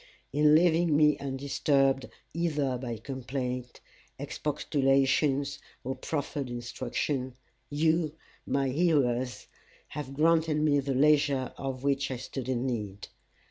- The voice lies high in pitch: No, low, 135 Hz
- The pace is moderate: No, slow, 110 wpm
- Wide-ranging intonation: No, narrow, 2.6 semitones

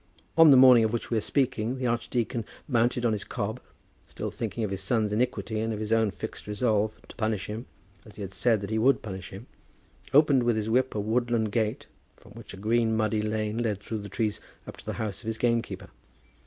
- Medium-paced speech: No, fast, 225 wpm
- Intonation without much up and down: Yes, narrow, 2.1 semitones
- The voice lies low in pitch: Yes, low, 110 Hz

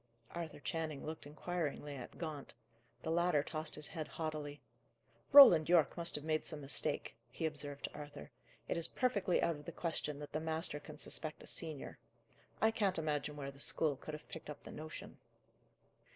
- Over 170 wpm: Yes, average, 180 wpm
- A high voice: No, medium, 155 Hz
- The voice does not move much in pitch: Yes, narrow, 2.1 semitones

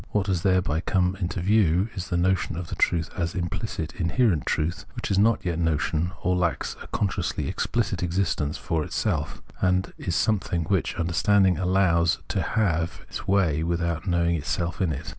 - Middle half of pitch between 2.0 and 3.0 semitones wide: Yes, narrow, 2.4 semitones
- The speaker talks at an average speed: Yes, average, 180 wpm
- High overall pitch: No, very low, 90 Hz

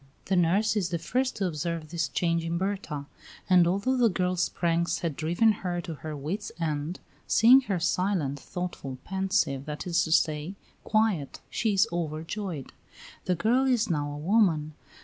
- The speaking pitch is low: No, medium, 175 Hz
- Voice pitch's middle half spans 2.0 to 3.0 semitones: No, average, 4.2 semitones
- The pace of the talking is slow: No, average, 170 wpm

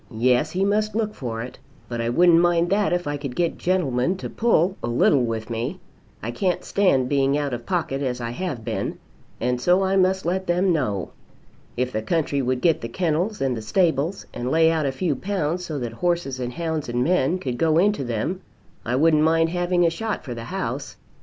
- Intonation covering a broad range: Yes, wide, 6.2 semitones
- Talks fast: Yes, fast, 215 wpm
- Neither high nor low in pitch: Yes, medium, 155 Hz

